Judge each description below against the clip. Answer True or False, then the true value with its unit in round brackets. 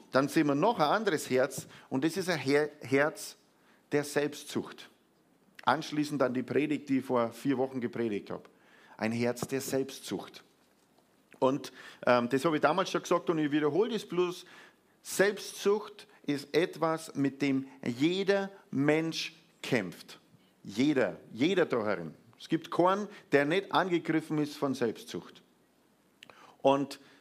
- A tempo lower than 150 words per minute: True (140 wpm)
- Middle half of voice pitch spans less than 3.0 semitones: False (3.9 semitones)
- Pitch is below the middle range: False (145 Hz)